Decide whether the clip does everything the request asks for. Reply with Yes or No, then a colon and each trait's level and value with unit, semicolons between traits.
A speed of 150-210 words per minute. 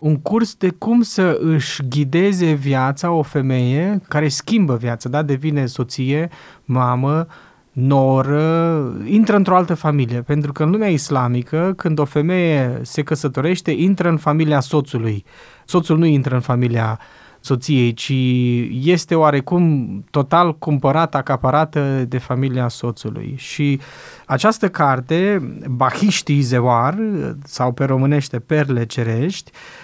No: average, 125 wpm